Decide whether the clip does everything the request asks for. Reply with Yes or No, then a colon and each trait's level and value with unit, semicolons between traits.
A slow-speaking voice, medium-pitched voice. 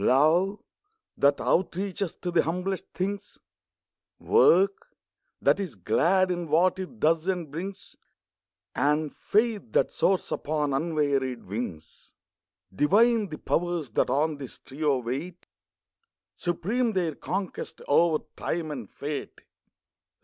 Yes: slow, 115 wpm; medium, 165 Hz